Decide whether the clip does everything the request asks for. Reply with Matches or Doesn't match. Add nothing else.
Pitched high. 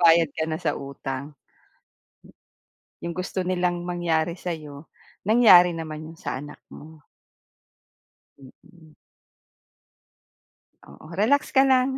Doesn't match